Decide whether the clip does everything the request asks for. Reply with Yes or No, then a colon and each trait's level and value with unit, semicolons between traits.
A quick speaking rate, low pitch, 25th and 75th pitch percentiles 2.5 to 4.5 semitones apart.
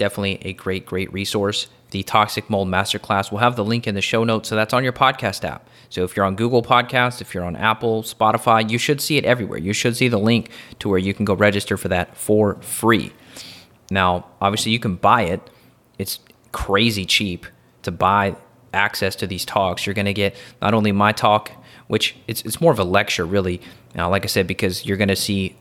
Yes: fast, 220 wpm; low, 100 Hz; average, 2.8 semitones